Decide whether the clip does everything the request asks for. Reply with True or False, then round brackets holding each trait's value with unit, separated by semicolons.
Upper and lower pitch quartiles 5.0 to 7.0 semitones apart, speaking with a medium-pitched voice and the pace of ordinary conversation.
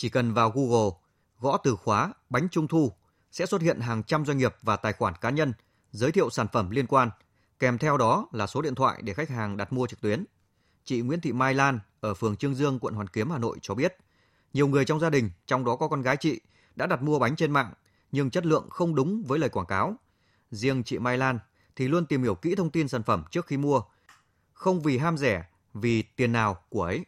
False (5.3 semitones; 125 Hz; 240 wpm)